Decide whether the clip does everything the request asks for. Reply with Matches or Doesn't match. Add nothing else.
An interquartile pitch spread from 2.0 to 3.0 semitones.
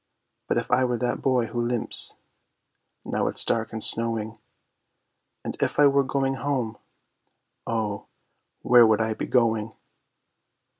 Matches